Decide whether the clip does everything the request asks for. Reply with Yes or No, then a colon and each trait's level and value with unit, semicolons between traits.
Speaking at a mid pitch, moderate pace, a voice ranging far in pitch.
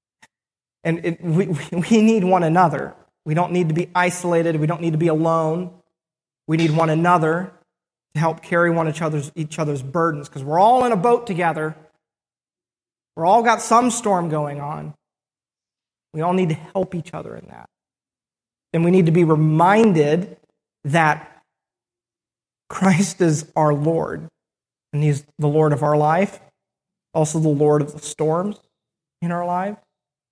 No: medium, 165 Hz; average, 160 wpm; narrow, 2.5 semitones